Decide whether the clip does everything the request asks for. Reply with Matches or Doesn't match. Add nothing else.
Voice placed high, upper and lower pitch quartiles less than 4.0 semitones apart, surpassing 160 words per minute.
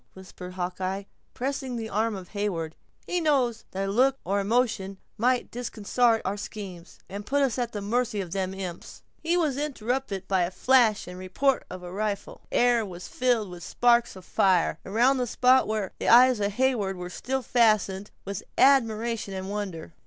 Doesn't match